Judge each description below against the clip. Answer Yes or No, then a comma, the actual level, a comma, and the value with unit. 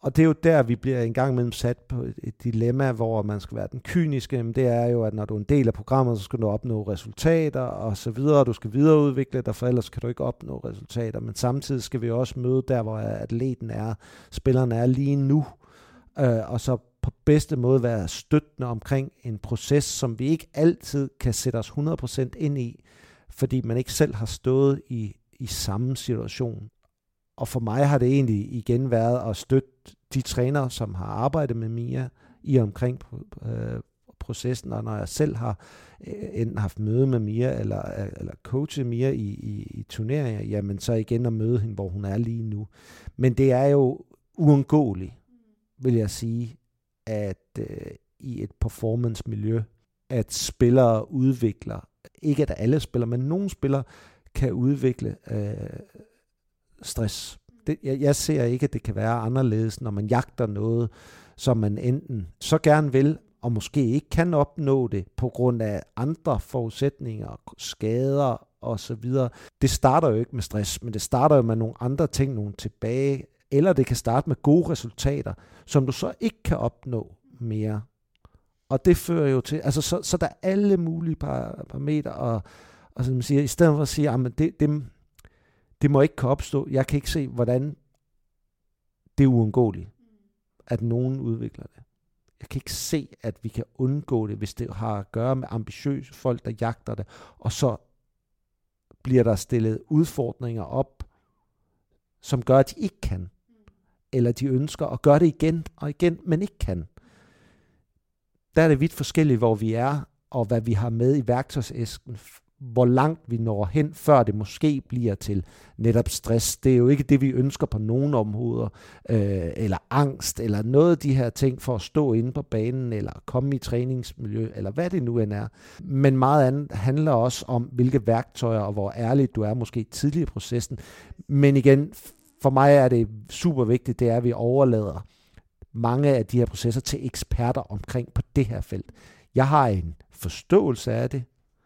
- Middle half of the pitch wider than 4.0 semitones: No, average, 3.7 semitones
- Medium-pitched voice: No, low, 125 Hz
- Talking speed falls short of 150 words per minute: No, average, 185 wpm